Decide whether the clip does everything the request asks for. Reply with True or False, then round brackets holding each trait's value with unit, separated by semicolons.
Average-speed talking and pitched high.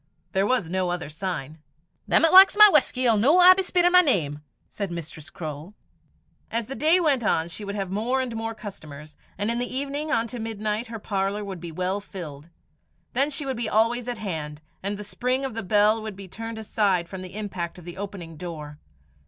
False (215 wpm; 205 Hz)